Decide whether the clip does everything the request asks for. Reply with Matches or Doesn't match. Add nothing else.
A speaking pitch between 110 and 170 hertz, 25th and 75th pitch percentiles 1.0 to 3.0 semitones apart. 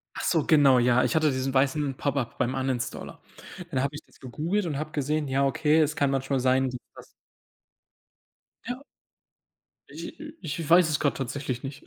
Matches